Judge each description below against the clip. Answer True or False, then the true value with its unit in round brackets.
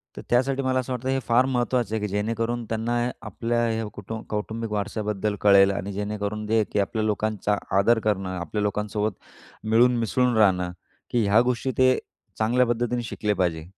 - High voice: False (110 Hz)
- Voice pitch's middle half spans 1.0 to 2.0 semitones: False (2.7 semitones)